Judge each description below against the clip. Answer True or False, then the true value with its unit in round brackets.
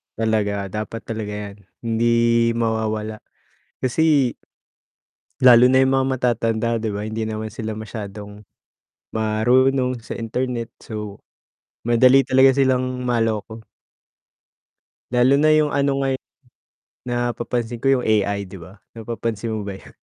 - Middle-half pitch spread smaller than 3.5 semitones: True (2.8 semitones)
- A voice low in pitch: True (115 Hz)